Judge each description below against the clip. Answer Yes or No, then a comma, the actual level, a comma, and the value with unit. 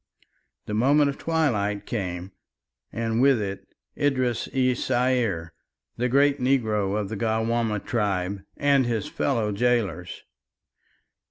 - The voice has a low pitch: Yes, low, 115 Hz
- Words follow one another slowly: Yes, slow, 115 wpm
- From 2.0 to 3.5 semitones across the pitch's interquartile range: No, average, 4.0 semitones